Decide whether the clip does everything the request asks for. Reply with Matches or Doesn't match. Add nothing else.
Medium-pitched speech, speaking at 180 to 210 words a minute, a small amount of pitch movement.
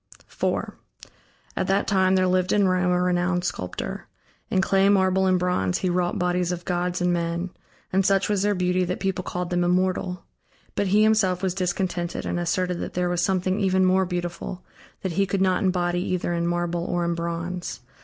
Matches